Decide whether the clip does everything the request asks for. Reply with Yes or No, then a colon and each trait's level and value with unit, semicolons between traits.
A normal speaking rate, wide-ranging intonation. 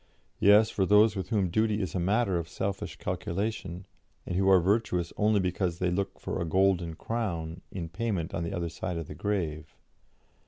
No: average, 185 wpm; average, 3.3 semitones